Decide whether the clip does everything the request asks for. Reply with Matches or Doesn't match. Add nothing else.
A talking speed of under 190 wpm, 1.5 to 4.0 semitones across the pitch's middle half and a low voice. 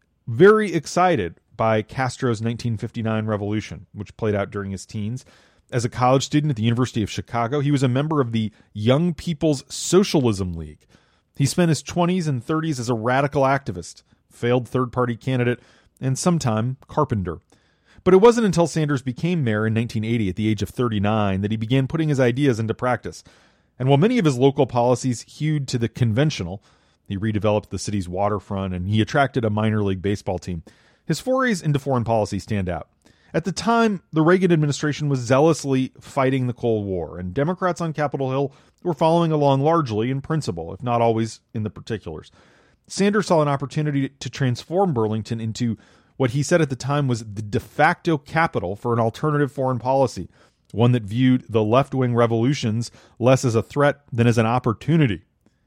Doesn't match